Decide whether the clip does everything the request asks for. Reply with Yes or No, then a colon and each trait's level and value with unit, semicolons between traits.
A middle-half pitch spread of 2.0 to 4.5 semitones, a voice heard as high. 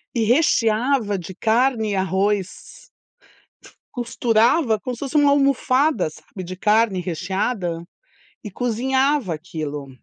No: wide, 5.4 semitones; high, 220 Hz